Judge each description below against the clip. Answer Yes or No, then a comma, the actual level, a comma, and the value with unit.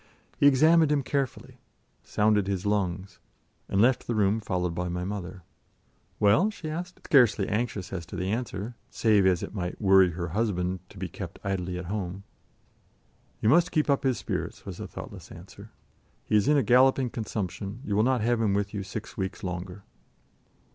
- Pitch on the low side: Yes, low, 105 Hz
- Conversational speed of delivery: Yes, average, 180 wpm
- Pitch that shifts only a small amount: No, average, 4.6 semitones